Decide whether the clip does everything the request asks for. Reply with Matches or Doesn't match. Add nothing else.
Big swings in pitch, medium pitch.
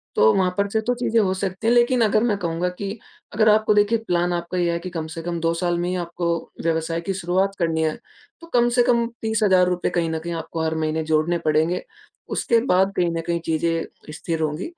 Doesn't match